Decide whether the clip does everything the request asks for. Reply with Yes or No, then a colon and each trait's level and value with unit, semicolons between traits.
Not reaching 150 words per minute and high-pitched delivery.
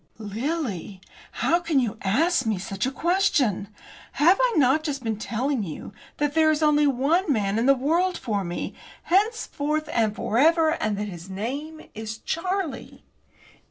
No: average, 160 wpm; very high, 275 Hz